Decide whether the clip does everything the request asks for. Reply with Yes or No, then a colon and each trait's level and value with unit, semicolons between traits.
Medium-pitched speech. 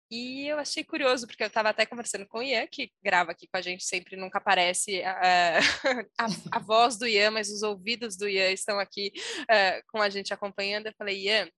No: high, 210 Hz